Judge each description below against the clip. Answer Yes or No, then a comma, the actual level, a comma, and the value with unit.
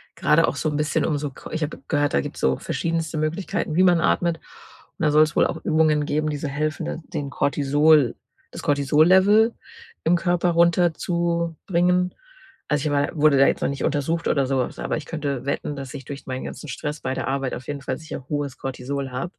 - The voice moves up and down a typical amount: Yes, average, 3.0 semitones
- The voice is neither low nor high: Yes, medium, 150 Hz